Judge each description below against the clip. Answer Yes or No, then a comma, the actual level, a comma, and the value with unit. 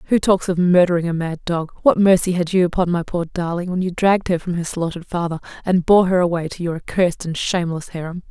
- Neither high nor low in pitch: Yes, medium, 175 Hz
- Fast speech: Yes, fast, 240 wpm